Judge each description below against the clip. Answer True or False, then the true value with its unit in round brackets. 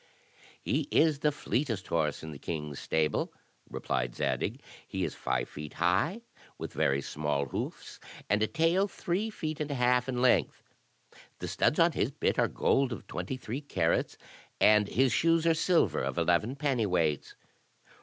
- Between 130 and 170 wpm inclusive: True (165 wpm)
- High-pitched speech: False (115 Hz)